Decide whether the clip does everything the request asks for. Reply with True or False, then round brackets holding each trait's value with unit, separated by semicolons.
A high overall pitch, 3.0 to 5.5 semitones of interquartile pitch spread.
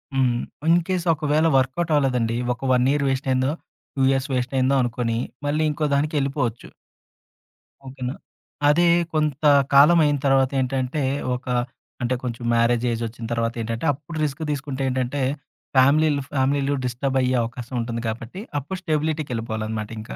False (130 Hz; 3.3 semitones)